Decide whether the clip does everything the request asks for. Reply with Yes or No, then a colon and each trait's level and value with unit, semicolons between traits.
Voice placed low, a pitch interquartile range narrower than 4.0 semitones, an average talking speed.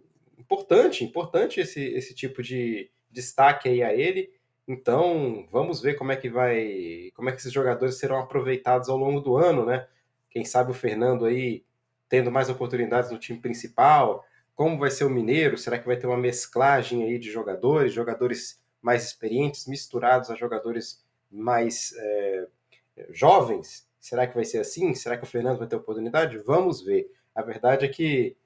Yes: low, 125 Hz; narrow, 2.4 semitones; average, 170 wpm